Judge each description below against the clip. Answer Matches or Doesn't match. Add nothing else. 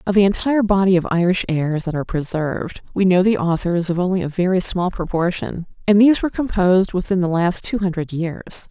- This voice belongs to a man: Doesn't match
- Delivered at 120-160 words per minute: Doesn't match